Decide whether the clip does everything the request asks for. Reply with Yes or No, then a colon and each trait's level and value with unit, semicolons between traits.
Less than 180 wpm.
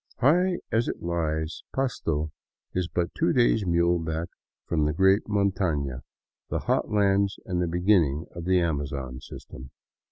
Yes: average, 140 wpm